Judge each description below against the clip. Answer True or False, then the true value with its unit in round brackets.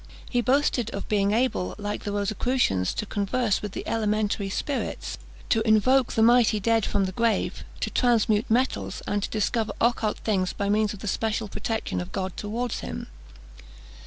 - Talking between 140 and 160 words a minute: False (170 wpm)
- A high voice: True (215 Hz)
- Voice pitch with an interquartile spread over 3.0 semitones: False (2.5 semitones)